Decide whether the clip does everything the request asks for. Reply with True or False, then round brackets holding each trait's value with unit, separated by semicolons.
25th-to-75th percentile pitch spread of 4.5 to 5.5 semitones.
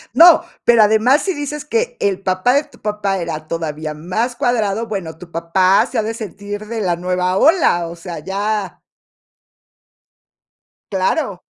True (4.9 semitones)